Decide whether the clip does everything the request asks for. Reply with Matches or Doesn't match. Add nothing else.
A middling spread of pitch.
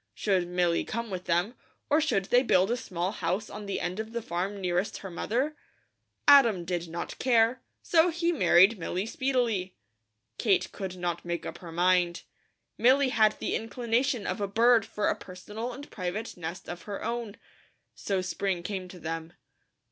Matches